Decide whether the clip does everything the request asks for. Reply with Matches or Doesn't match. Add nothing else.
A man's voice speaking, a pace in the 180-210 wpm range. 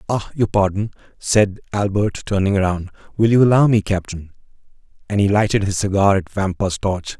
Doesn't match